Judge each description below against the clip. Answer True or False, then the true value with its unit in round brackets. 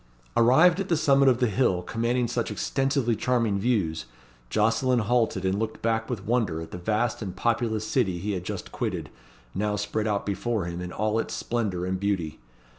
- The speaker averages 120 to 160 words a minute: False (190 wpm)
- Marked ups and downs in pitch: False (3.7 semitones)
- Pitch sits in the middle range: False (110 Hz)